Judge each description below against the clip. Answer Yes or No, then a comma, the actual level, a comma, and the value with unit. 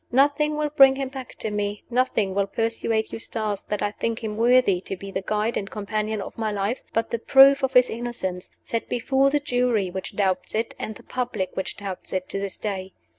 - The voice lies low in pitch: No, high, 220 Hz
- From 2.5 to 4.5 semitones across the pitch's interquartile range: Yes, average, 3.9 semitones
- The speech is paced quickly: Yes, fast, 215 wpm